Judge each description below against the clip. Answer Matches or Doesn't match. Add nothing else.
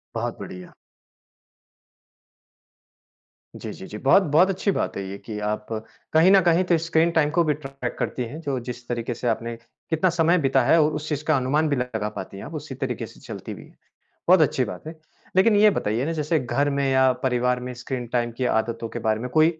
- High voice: Doesn't match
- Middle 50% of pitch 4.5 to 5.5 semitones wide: Matches